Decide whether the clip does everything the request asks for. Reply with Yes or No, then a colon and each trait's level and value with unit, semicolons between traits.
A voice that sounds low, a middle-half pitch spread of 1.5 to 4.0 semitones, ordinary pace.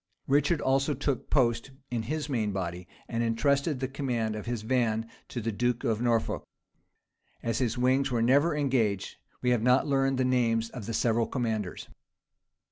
Yes: low, 120 Hz; average, 3.0 semitones; average, 170 wpm